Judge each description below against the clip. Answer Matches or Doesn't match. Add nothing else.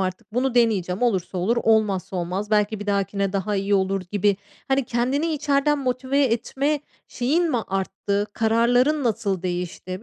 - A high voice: Matches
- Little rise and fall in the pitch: Doesn't match